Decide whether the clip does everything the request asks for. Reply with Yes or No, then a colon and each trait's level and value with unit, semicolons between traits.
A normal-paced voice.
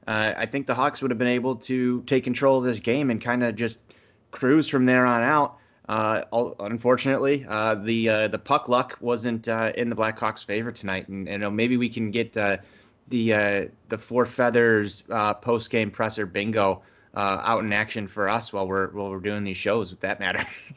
No: fast, 215 wpm